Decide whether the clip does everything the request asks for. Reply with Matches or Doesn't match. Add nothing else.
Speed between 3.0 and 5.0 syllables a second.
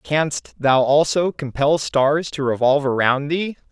Matches